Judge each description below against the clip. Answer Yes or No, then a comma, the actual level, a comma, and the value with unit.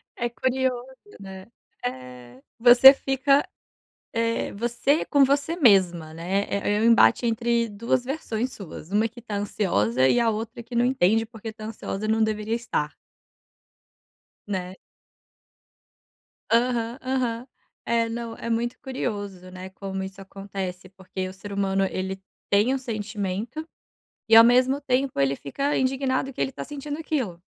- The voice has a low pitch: No, high, 225 Hz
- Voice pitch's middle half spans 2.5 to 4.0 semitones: No, average, 4.5 semitones